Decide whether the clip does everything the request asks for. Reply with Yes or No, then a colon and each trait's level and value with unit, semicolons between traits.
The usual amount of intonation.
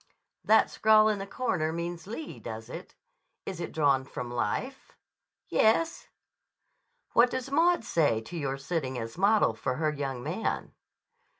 No: wide, 8.5 semitones